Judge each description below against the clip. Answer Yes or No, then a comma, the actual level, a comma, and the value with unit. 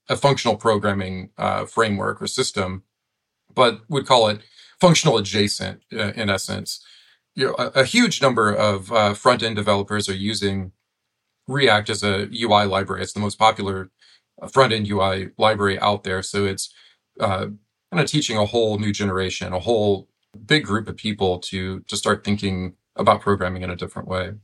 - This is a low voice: Yes, low, 105 Hz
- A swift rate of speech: No, average, 170 wpm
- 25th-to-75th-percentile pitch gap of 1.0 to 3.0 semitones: Yes, narrow, 2.5 semitones